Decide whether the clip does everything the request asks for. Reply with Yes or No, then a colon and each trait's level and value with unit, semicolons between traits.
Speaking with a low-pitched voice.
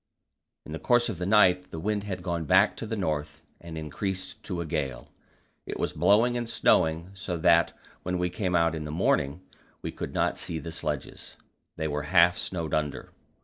Yes: very low, 85 Hz